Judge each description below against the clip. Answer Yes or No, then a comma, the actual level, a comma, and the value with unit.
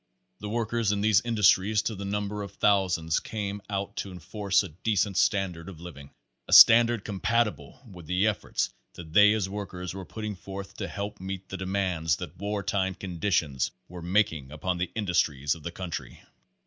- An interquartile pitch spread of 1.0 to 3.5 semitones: Yes, average, 2.7 semitones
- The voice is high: No, very low, 95 Hz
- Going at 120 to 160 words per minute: No, average, 175 wpm